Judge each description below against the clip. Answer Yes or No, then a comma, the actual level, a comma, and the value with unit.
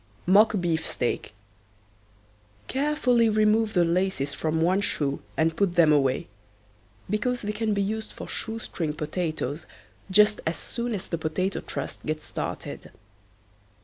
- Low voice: No, medium, 185 Hz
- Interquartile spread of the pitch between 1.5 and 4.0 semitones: No, average, 5.3 semitones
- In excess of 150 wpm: No, slow, 135 wpm